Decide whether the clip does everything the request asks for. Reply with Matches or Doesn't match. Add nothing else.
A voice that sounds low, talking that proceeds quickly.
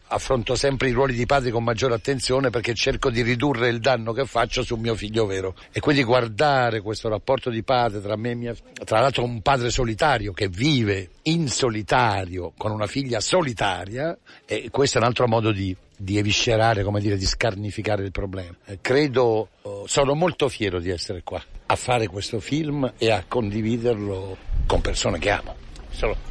Matches